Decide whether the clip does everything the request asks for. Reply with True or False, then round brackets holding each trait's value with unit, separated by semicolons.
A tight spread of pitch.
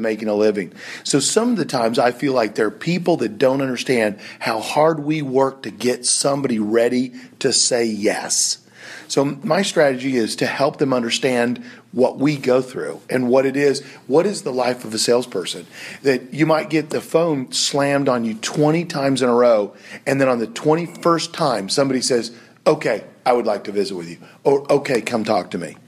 False (3.7 semitones)